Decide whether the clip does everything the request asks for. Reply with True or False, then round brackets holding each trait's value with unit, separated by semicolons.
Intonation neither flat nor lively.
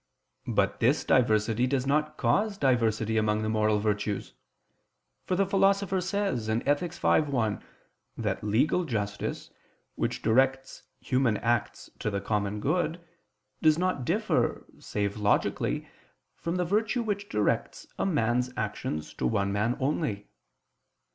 False (7.9 semitones)